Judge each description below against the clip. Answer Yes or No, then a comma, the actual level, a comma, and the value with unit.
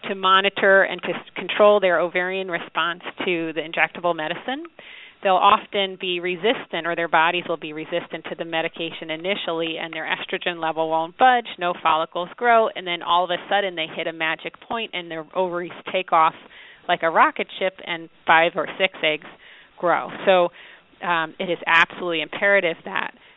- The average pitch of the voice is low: No, medium, 175 Hz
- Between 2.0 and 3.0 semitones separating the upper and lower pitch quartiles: Yes, narrow, 2.6 semitones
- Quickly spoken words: No, average, 175 wpm